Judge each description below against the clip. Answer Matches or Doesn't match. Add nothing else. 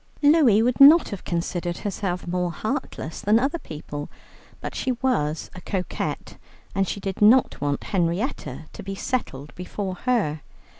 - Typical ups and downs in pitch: Doesn't match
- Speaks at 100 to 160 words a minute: Matches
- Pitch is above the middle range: Matches